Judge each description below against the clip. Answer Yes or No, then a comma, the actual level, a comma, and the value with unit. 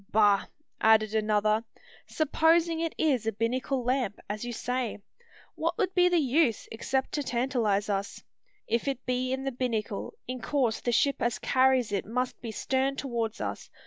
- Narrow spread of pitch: No, average, 3.6 semitones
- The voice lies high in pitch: Yes, very high, 250 Hz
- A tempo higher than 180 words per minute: No, average, 170 wpm